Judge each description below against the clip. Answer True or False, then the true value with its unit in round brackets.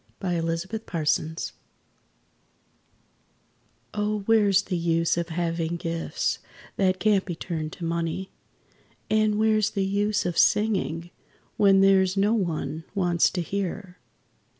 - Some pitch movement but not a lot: True (3.4 semitones)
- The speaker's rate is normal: False (120 wpm)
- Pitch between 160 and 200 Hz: True (185 Hz)